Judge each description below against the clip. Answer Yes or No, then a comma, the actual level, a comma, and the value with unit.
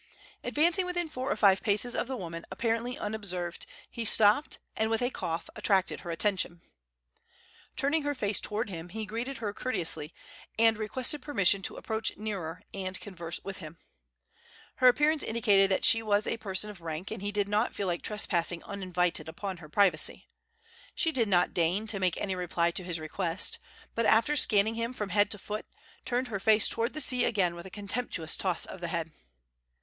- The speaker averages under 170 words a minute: No, average, 185 wpm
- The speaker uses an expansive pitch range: No, average, 4.2 semitones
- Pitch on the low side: No, high, 205 Hz